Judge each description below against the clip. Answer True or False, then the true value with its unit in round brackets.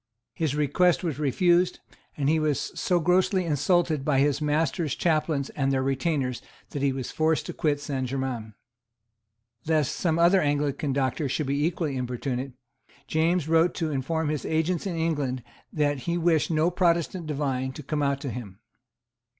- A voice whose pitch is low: False (150 Hz)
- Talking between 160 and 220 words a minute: True (165 wpm)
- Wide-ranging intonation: False (3.3 semitones)